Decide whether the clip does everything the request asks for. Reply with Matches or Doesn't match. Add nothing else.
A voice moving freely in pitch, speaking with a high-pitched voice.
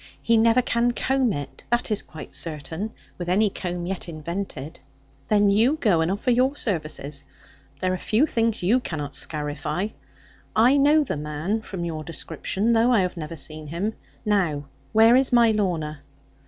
Matches